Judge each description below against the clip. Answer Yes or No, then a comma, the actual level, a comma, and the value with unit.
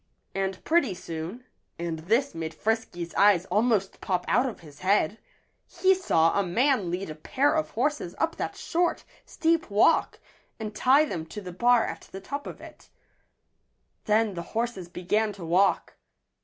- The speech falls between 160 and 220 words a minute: Yes, average, 165 wpm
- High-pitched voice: Yes, high, 205 Hz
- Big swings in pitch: Yes, wide, 6.2 semitones